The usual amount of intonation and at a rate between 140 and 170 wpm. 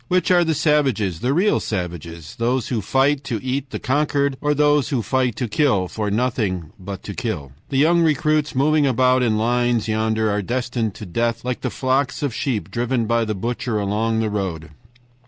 No: average, 4.6 semitones; average, 190 wpm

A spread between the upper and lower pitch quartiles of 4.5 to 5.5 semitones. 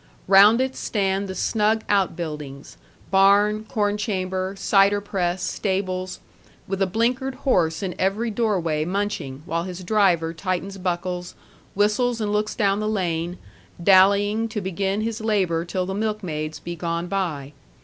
No: average, 2.9 semitones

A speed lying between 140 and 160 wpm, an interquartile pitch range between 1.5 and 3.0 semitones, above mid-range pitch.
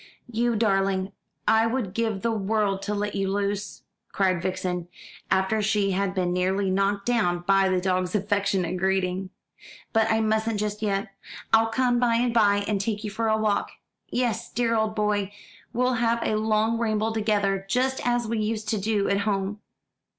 No: average, 175 wpm; narrow, 2.4 semitones; high, 210 Hz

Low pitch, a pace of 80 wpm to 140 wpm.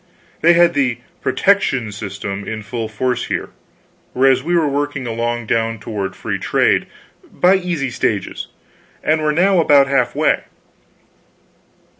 Yes: low, 130 Hz; slow, 135 wpm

